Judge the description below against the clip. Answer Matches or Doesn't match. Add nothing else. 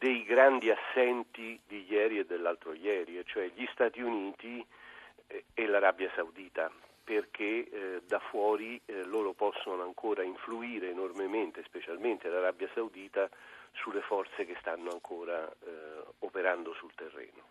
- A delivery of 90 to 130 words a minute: Matches